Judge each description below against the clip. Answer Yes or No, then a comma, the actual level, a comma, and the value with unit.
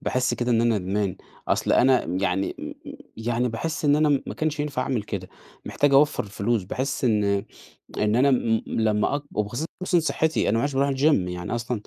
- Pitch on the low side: Yes, low, 120 Hz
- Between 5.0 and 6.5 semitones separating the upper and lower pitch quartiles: Yes, average, 5.3 semitones